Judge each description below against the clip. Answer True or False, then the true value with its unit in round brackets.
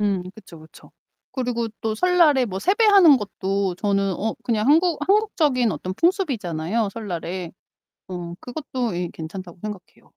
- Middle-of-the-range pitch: False (215 Hz)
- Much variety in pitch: True (7.6 semitones)